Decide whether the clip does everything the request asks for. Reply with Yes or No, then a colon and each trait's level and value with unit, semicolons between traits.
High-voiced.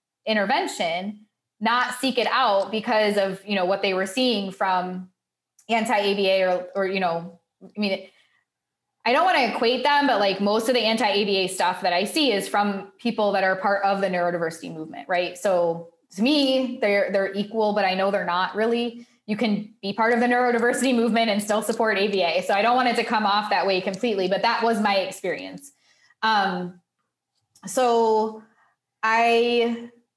Yes: high, 210 Hz